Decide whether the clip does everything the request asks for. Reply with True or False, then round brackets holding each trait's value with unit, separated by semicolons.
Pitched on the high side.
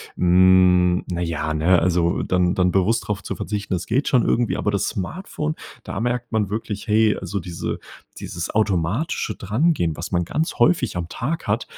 False (95 Hz)